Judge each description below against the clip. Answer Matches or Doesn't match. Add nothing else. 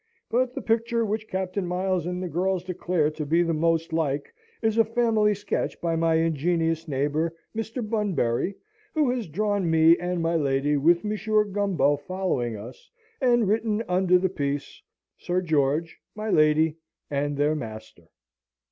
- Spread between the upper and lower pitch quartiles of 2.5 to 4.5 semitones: Doesn't match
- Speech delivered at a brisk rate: Doesn't match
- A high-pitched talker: Doesn't match